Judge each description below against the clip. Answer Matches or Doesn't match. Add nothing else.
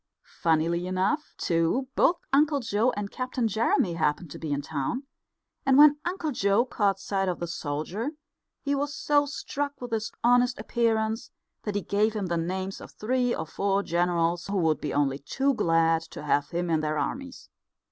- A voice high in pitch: Matches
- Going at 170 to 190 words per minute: Matches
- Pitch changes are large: Matches